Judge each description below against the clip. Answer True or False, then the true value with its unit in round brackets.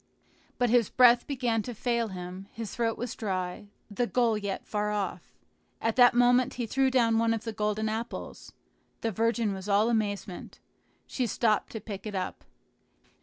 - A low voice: False (225 Hz)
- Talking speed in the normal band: True (170 wpm)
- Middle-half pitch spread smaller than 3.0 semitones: True (2.5 semitones)